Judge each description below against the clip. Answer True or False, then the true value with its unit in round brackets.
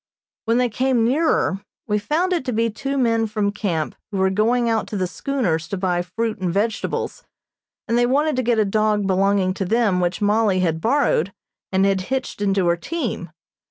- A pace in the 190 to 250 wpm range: True (195 wpm)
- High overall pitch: True (215 Hz)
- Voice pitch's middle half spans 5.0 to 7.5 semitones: False (4.2 semitones)